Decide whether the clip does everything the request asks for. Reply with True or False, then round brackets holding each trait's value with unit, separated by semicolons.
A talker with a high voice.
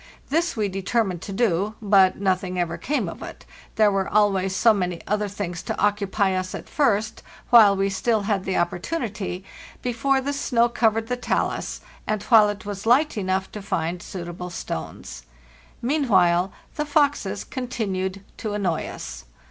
True (200 Hz)